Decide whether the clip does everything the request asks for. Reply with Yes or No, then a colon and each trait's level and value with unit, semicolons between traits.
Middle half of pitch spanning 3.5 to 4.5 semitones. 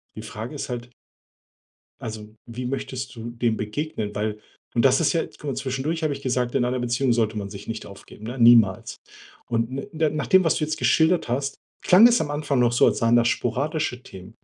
Yes: average, 4.1 semitones